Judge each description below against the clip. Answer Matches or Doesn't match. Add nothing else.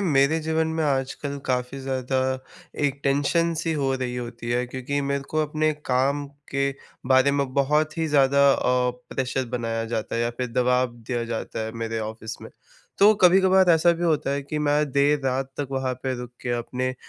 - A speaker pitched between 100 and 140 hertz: Matches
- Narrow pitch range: Doesn't match